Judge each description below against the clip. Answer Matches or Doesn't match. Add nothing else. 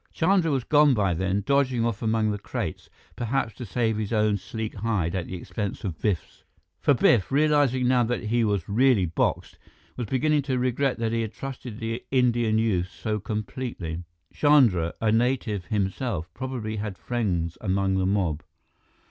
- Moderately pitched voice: Doesn't match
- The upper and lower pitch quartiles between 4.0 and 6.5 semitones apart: Matches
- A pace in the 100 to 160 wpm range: Doesn't match